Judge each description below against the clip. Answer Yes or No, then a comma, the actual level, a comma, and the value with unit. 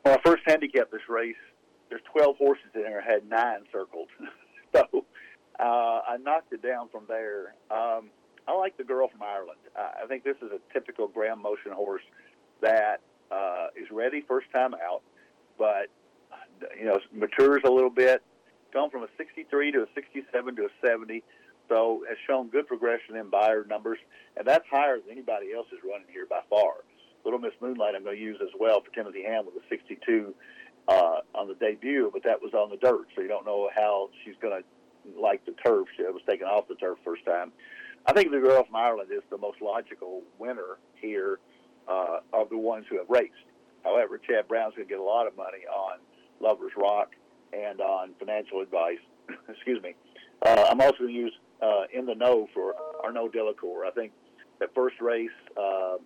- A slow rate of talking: No, average, 195 wpm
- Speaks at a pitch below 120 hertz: No, medium, 140 Hz